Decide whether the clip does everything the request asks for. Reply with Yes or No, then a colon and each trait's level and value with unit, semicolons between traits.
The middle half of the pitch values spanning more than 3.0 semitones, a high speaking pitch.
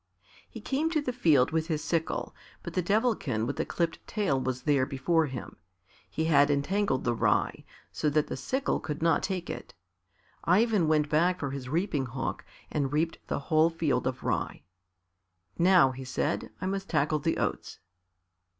No: average, 4.7 semitones; medium, 155 Hz